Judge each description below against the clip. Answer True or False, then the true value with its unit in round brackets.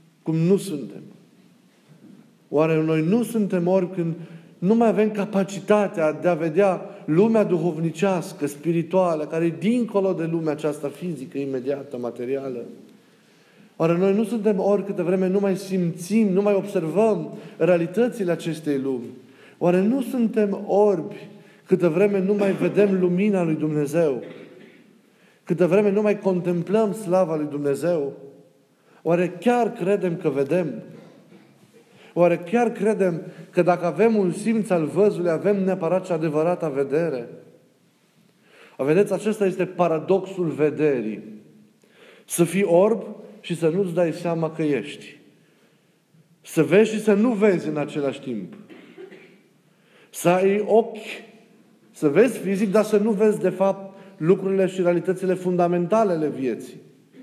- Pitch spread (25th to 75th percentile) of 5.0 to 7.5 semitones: False (3.8 semitones)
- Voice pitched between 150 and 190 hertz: True (185 Hz)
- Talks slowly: False (135 wpm)